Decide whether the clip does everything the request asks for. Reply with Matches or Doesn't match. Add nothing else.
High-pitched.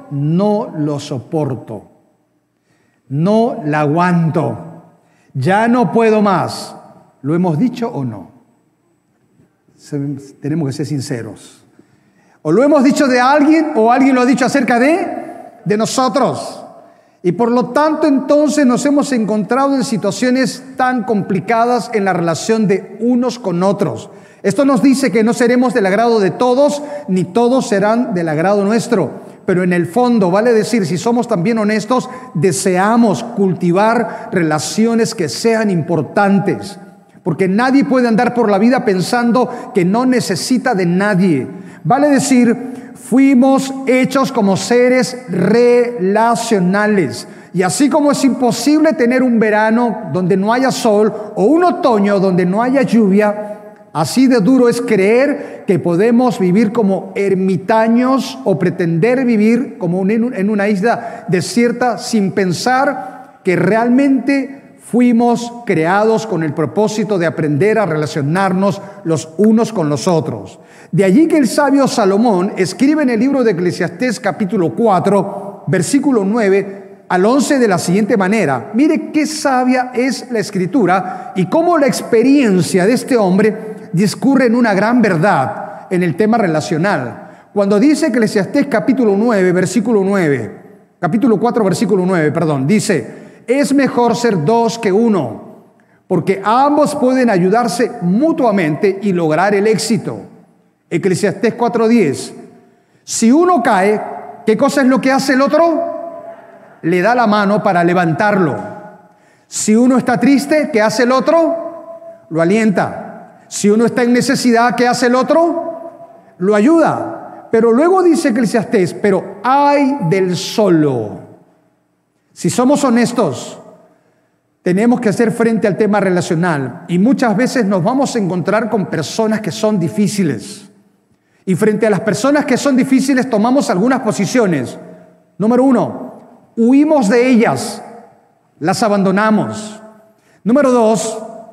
Matches